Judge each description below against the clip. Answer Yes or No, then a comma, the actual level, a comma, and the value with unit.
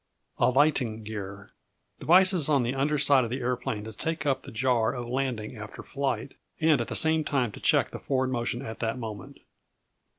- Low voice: Yes, low, 125 Hz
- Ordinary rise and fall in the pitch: Yes, average, 3.9 semitones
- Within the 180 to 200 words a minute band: Yes, average, 190 wpm